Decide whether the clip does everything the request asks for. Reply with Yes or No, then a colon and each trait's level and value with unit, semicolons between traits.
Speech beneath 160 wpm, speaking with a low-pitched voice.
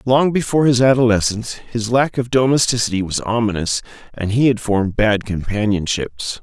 Yes: average, 150 wpm; low, 115 Hz